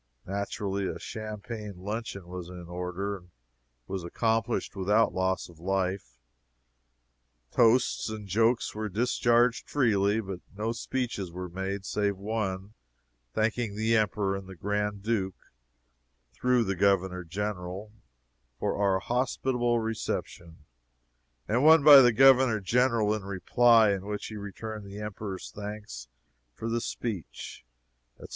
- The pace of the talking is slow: Yes, slow, 130 wpm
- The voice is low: Yes, low, 105 Hz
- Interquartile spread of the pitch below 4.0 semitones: Yes, average, 3.0 semitones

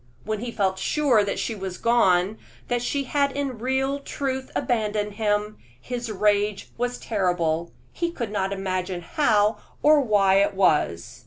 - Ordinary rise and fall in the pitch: Yes, average, 4.3 semitones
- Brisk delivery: No, average, 155 wpm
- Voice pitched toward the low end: No, high, 210 Hz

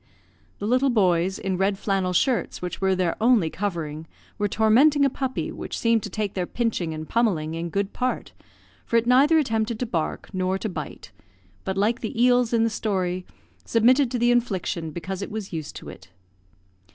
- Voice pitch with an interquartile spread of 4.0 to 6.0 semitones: Yes, average, 4.5 semitones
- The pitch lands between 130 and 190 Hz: No, high, 205 Hz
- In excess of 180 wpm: Yes, average, 190 wpm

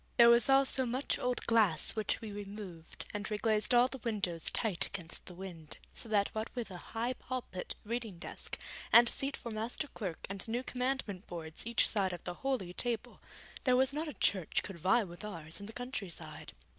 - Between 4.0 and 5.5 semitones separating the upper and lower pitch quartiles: Yes, average, 4.7 semitones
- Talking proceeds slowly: No, average, 195 wpm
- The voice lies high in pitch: Yes, high, 215 Hz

